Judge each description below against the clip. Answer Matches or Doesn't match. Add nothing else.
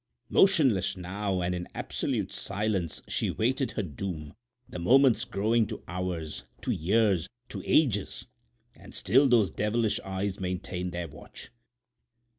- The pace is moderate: Doesn't match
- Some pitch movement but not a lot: Matches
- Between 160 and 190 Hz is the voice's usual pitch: Doesn't match